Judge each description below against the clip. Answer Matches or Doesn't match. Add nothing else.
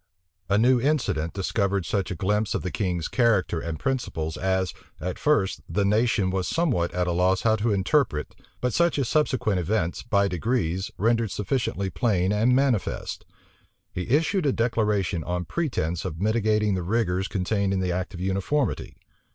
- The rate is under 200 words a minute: Matches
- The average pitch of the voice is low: Matches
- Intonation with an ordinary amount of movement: Matches